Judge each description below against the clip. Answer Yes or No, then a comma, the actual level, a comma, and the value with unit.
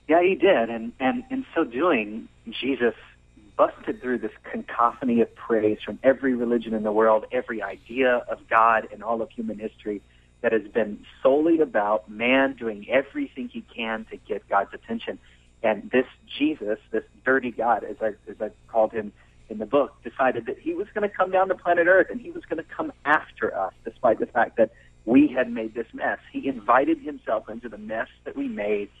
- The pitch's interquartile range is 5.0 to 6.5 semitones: Yes, wide, 5.5 semitones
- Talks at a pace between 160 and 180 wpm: No, average, 200 wpm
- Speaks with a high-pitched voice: No, low, 120 Hz